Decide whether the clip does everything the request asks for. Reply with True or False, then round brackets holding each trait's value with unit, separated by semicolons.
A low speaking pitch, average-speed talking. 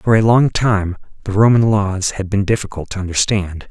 True (100 Hz; 195 wpm)